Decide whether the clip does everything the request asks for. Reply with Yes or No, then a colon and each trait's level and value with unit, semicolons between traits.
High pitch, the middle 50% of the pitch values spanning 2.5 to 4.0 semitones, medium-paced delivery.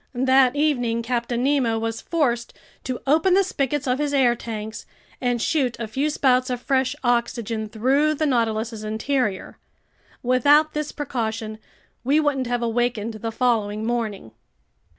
Yes: high, 245 Hz; average, 3.4 semitones; average, 145 wpm